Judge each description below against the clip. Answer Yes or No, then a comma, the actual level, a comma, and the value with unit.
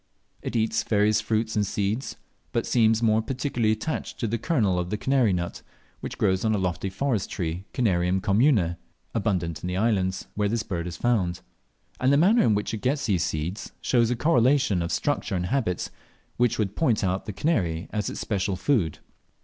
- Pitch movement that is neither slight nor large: Yes, average, 4.2 semitones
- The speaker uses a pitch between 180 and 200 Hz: No, low, 105 Hz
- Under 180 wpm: No, average, 195 wpm